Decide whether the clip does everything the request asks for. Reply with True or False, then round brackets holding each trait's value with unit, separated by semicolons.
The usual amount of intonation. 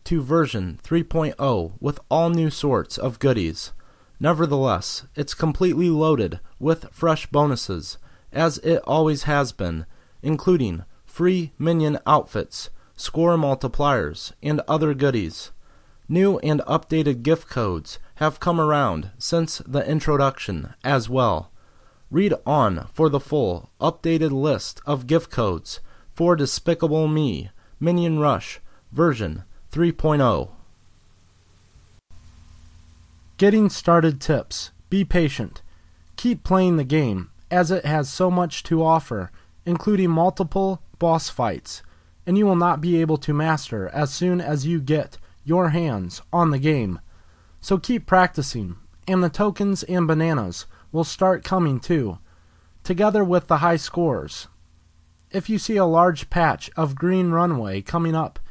False (8.9 semitones)